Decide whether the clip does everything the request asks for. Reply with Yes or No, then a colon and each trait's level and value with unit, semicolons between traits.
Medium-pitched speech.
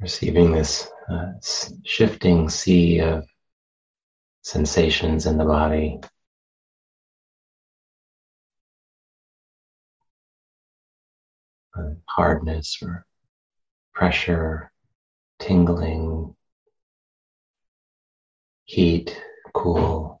No: very low, 80 Hz